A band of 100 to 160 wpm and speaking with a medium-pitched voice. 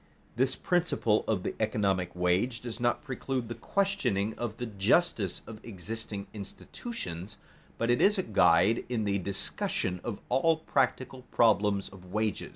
No: average, 150 wpm; low, 110 Hz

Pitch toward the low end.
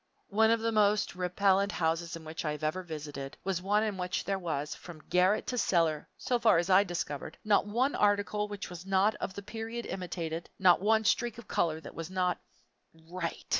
No: medium, 185 Hz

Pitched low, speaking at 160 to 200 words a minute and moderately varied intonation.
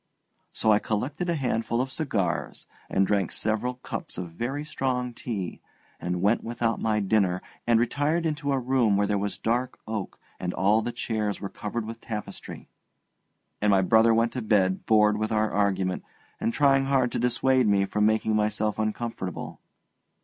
Yes: low, 110 Hz; average, 170 wpm; average, 3.3 semitones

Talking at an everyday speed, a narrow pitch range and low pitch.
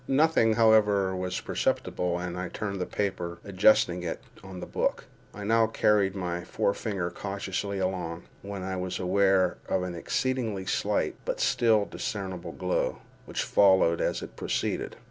Yes: average, 155 wpm; narrow, 2.2 semitones; very low, 95 Hz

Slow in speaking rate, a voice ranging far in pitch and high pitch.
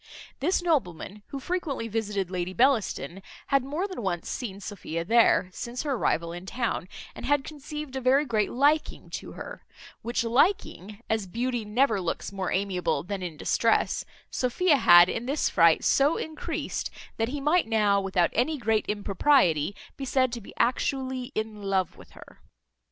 No: average, 165 wpm; wide, 6.1 semitones; high, 230 Hz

